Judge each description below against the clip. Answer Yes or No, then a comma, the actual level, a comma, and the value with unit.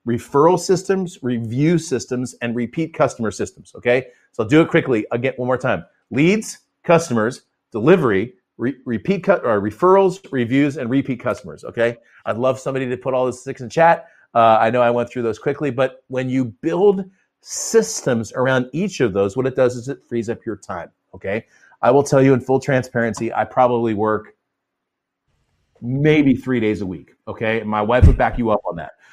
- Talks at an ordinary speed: Yes, average, 190 wpm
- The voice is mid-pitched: No, low, 130 Hz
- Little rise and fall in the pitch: No, average, 4.1 semitones